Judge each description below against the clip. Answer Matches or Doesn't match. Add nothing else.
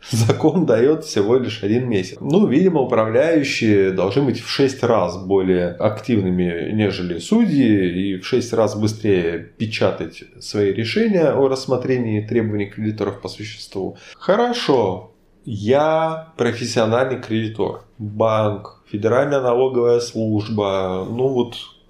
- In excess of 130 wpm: Doesn't match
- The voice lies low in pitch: Matches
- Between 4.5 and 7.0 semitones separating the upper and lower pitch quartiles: Doesn't match